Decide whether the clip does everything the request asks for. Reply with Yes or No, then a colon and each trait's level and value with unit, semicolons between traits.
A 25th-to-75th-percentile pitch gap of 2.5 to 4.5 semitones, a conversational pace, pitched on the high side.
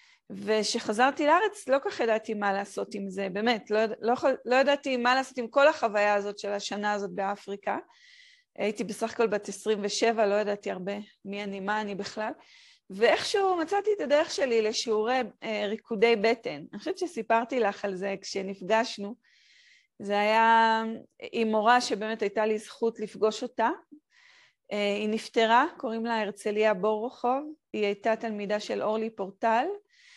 No: average, 4.0 semitones; fast, 155 wpm; high, 225 Hz